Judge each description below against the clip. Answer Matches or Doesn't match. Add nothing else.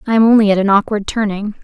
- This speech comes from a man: Doesn't match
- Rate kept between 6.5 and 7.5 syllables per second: Matches